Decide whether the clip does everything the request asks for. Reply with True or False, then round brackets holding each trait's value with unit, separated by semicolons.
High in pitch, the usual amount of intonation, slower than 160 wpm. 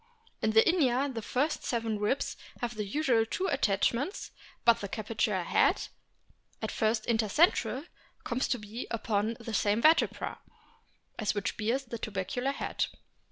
True (230 Hz; 3.4 semitones; 150 wpm)